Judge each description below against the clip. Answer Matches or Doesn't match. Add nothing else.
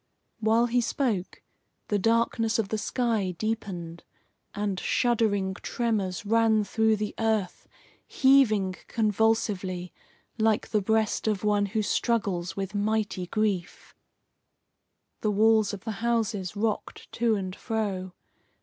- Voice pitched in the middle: Doesn't match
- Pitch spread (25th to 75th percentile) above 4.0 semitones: Doesn't match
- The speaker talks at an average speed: Doesn't match